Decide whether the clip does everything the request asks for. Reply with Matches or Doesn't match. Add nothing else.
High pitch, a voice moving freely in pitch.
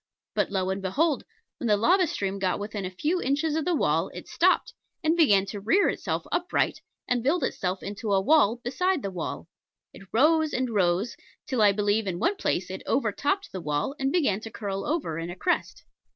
Matches